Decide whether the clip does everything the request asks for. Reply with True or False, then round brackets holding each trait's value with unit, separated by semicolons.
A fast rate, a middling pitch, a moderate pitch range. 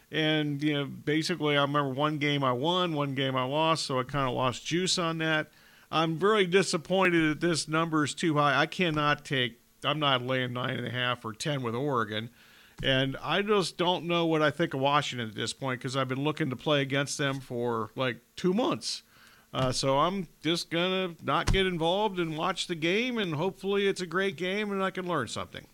True (215 wpm; 150 Hz; 4.7 semitones)